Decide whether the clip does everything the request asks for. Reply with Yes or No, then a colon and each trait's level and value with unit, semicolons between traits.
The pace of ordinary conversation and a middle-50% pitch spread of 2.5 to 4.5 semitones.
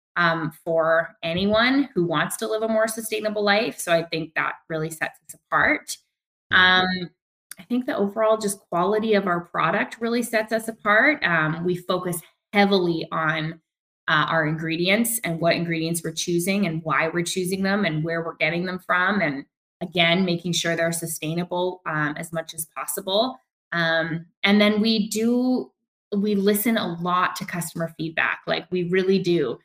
Yes: average, 170 wpm; average, 3.9 semitones